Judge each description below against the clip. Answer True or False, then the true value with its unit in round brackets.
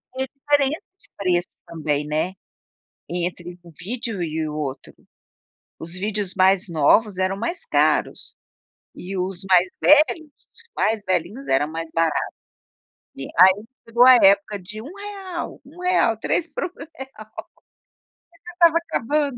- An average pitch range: False (7.9 semitones)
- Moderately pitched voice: False (200 Hz)